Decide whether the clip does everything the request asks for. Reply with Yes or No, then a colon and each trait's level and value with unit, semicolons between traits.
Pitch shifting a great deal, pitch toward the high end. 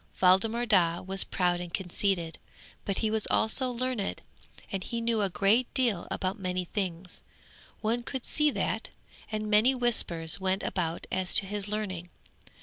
No: average, 3.8 semitones; high, 200 Hz